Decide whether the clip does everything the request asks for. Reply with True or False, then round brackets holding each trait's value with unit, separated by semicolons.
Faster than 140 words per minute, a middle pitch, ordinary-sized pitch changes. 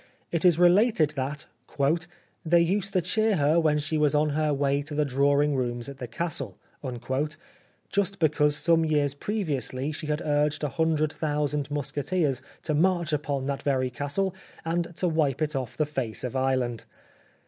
True (170 wpm; 150 Hz; 3.0 semitones)